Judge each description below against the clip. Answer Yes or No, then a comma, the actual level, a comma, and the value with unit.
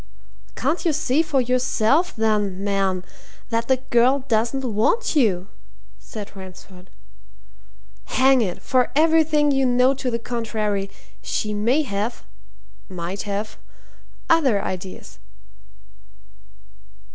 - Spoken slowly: Yes, slow, 110 wpm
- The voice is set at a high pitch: Yes, high, 230 Hz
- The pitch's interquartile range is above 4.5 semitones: Yes, average, 5.1 semitones